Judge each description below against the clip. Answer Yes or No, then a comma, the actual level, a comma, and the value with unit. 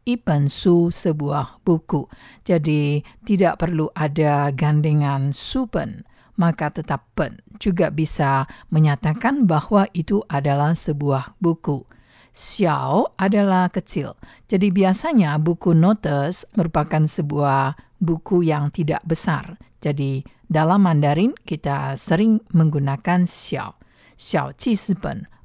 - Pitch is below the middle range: No, medium, 160 Hz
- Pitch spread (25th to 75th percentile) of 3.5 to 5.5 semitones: Yes, average, 4.4 semitones